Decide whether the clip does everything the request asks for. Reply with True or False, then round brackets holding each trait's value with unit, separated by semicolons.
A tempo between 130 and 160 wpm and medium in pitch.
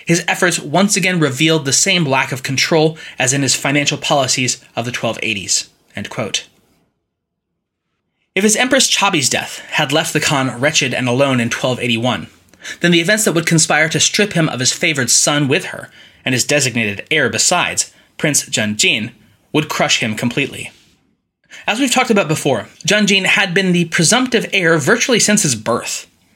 False (170 wpm; 155 Hz)